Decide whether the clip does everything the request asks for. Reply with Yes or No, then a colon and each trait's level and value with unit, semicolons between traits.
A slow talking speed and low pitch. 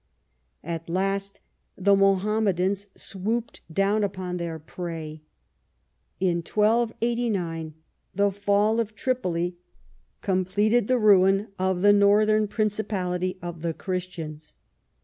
No: slow, 100 wpm; high, 195 Hz